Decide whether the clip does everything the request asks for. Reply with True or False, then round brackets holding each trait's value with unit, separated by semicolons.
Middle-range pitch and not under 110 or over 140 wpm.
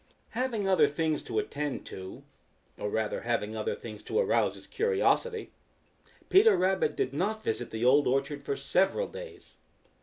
False (155 Hz; 155 wpm)